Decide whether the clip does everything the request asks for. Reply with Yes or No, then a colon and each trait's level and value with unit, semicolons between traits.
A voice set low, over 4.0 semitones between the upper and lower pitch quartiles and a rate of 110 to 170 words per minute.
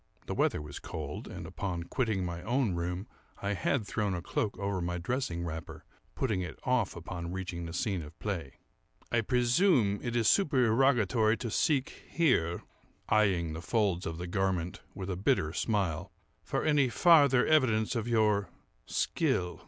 Yes: low, 100 Hz; wide, 5.6 semitones; average, 160 wpm